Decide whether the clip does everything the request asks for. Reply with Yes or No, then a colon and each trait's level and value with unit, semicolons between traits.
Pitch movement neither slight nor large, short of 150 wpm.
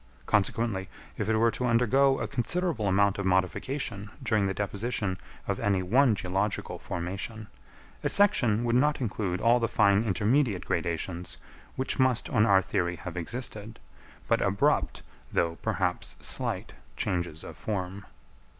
Yes: average, 4.0 semitones; average, 140 wpm